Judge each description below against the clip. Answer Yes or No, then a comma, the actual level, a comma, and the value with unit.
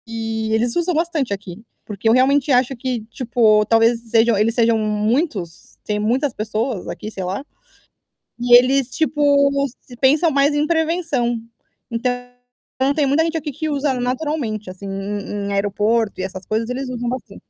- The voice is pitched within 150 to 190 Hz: No, high, 235 Hz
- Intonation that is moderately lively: Yes, average, 4.4 semitones